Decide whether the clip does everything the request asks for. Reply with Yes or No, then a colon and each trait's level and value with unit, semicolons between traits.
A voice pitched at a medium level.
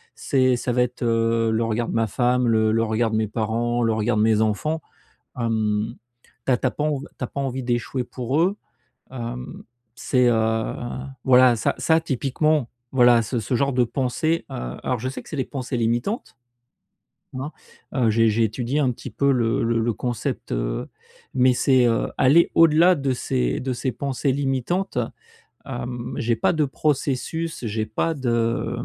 No: low, 120 Hz